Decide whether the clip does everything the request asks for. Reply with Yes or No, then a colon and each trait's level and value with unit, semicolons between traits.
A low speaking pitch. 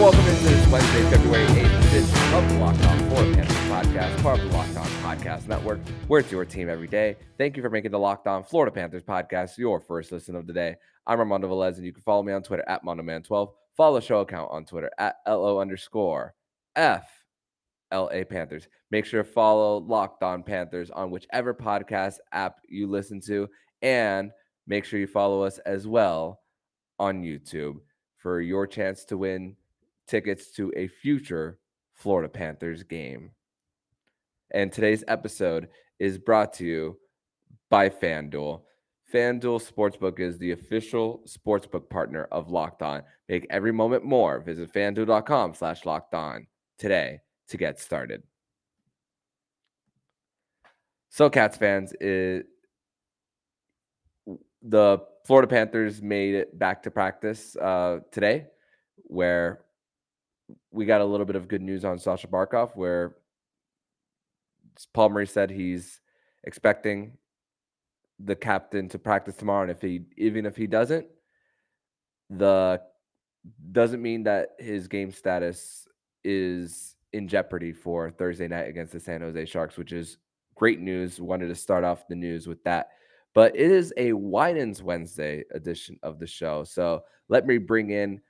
Yes: very low, 95 Hz